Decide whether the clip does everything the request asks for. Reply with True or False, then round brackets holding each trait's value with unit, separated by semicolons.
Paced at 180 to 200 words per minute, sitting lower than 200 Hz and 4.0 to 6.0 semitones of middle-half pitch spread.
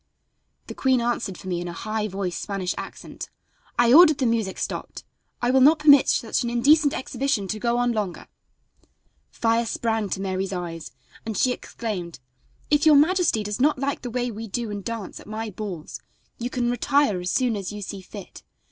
False (190 wpm; 225 Hz; 4.3 semitones)